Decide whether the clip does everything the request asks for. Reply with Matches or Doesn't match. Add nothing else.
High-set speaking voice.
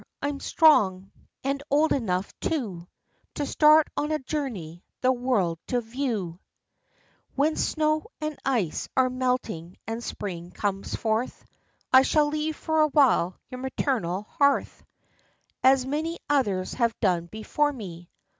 Matches